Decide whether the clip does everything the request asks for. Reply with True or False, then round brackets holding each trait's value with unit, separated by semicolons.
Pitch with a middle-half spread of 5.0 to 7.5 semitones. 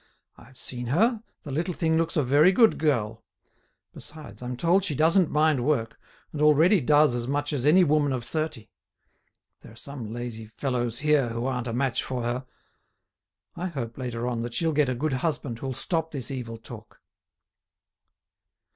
False (4.4 semitones)